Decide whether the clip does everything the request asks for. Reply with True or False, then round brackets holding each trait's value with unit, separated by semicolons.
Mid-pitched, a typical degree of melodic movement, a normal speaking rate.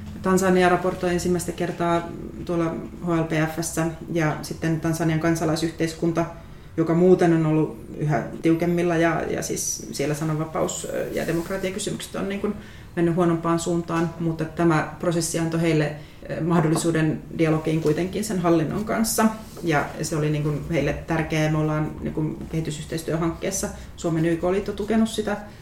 False (165 Hz; 1.8 semitones; 130 wpm)